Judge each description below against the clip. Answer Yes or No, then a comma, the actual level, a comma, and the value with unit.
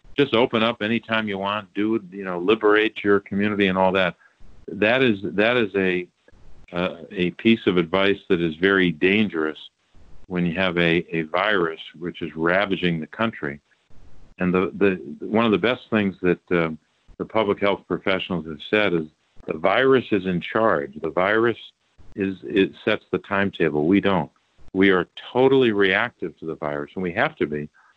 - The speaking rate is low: No, average, 180 wpm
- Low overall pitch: Yes, very low, 95 Hz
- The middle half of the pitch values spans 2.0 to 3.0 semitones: No, average, 3.5 semitones